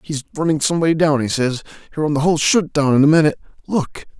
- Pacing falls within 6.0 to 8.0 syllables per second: Yes, 7.0 syllables/s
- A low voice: No, medium, 150 Hz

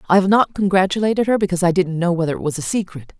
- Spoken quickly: Yes, fast, 265 wpm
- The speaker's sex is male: No, female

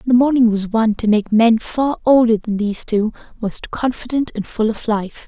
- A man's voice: No, female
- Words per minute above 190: Yes, fast, 205 wpm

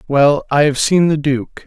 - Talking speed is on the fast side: Yes, fast, 215 wpm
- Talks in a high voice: No, medium, 145 Hz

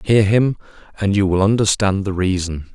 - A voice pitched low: Yes, low, 100 Hz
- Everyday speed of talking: Yes, average, 175 wpm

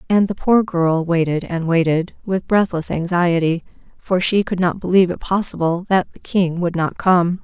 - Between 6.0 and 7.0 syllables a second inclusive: No, 4.8 syllables/s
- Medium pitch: Yes, medium, 175 Hz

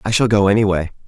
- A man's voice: Yes, male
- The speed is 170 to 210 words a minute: No, fast, 225 wpm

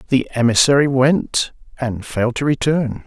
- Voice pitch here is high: No, low, 130 Hz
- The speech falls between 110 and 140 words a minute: Yes, slow, 135 wpm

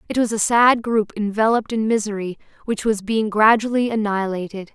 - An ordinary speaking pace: Yes, average, 165 wpm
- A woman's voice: Yes, female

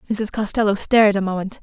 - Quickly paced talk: No, average, 185 wpm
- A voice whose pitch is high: Yes, high, 205 Hz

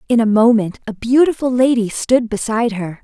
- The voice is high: Yes, high, 230 Hz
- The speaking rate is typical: Yes, average, 180 wpm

